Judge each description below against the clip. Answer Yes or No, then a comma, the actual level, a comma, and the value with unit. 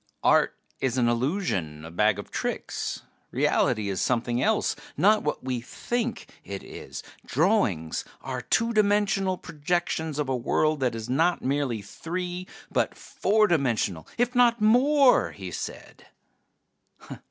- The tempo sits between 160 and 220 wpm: No, slow, 135 wpm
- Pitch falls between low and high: Yes, medium, 145 Hz